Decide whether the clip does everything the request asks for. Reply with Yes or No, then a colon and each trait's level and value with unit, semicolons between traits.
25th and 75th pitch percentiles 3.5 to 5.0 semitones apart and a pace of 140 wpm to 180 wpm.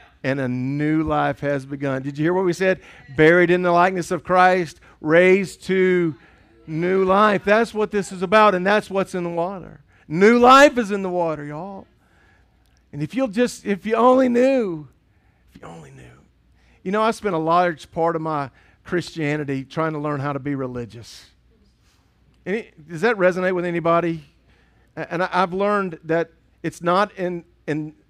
Yes: average, 4.2 semitones; average, 175 wpm